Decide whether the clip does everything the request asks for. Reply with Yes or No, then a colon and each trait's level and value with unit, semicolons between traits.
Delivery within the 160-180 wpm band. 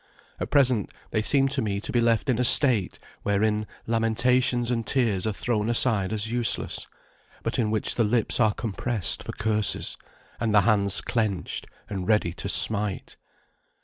Yes: average, 165 wpm